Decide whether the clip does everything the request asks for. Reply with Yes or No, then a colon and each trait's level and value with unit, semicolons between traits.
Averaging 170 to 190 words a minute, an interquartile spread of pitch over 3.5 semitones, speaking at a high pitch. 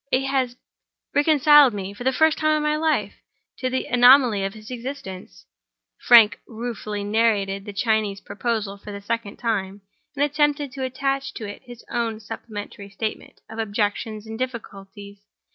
No: average, 160 wpm; average, 4.4 semitones; high, 230 Hz